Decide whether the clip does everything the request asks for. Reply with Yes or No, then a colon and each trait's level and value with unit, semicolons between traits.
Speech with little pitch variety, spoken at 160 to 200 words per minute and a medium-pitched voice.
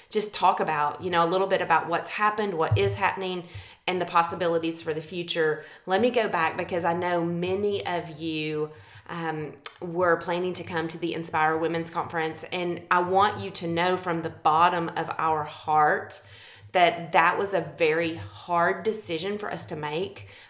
Yes: narrow, 2.2 semitones; average, 185 wpm; medium, 170 Hz